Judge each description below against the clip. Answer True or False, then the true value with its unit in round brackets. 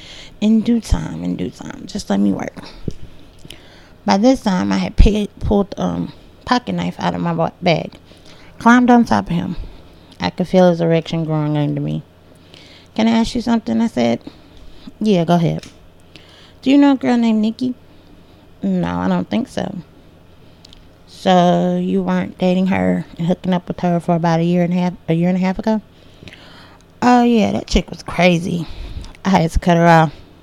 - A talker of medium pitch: True (175 Hz)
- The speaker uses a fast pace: False (185 wpm)